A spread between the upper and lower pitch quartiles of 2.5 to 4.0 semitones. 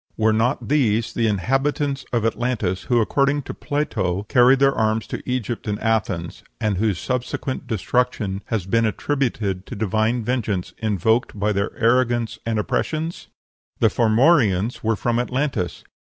Yes: average, 3.3 semitones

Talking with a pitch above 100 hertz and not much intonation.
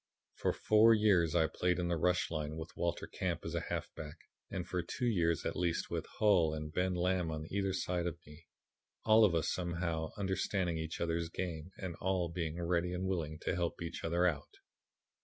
No: very low, 85 Hz; narrow, 2.1 semitones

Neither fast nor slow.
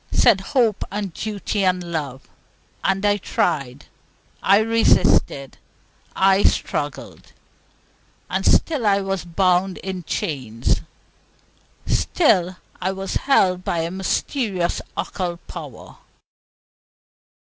No: slow, 100 wpm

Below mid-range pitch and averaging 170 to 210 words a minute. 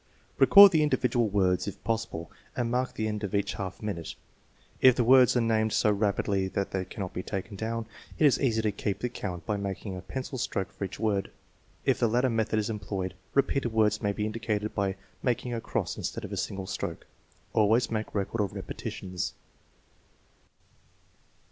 Yes: low, 105 Hz; average, 185 wpm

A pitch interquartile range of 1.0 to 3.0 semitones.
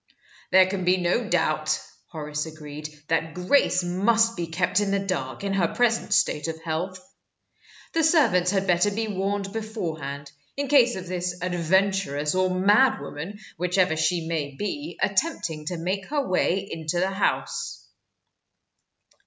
No: average, 3.6 semitones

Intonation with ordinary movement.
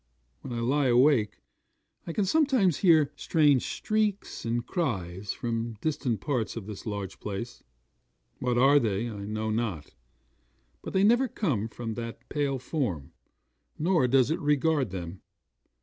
No: wide, 6.0 semitones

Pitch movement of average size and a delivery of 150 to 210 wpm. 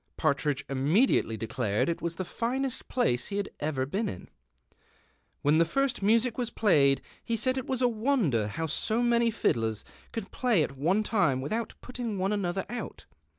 No: wide, 8.9 semitones; average, 175 wpm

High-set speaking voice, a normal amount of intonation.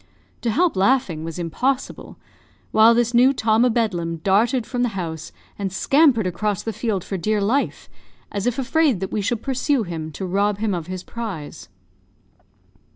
Yes: high, 215 Hz; average, 4.8 semitones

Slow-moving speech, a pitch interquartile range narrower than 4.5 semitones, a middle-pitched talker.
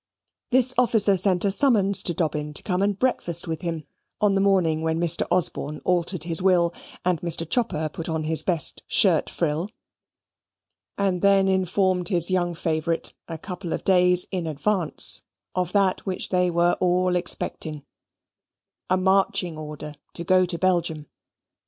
No: average, 160 wpm; narrow, 2.6 semitones; medium, 180 Hz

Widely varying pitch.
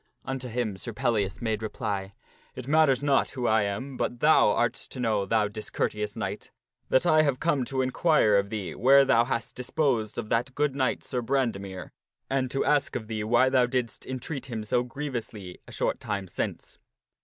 No: average, 3.8 semitones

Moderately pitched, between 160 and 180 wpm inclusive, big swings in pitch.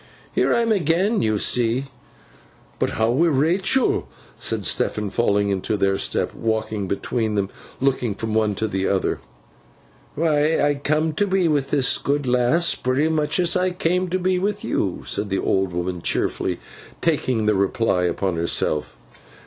No: low, 125 Hz; average, 170 wpm; wide, 8.1 semitones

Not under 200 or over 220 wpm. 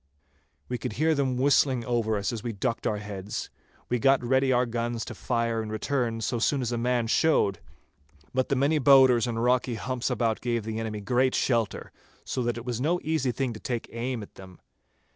Yes: fast, 205 wpm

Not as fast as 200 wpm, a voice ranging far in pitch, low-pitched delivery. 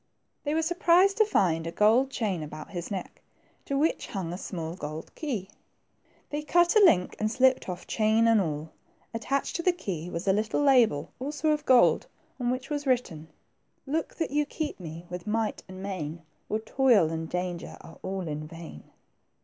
No: average, 190 wpm; wide, 8.4 semitones; high, 215 Hz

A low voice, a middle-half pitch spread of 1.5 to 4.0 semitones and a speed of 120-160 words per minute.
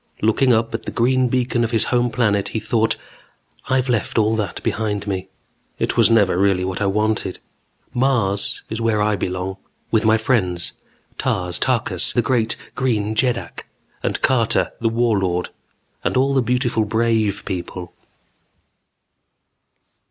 Yes: low, 110 Hz; average, 3.3 semitones; average, 145 wpm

